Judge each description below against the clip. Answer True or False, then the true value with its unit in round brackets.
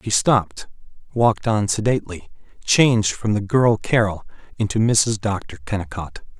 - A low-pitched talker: True (105 Hz)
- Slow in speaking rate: True (130 wpm)